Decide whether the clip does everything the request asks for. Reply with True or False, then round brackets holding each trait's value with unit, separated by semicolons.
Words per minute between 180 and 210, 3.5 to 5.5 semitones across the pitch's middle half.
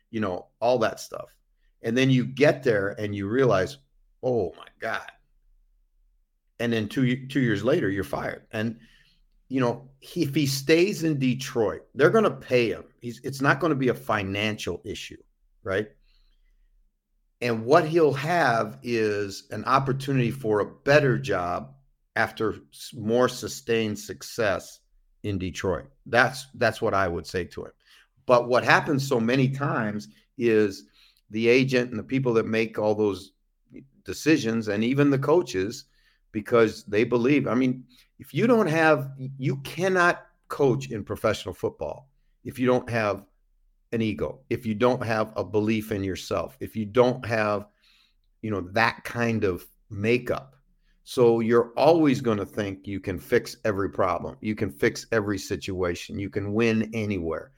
False (160 wpm; 4.0 semitones)